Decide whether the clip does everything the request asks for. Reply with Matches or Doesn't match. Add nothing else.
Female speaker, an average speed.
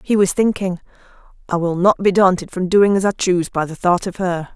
Doesn't match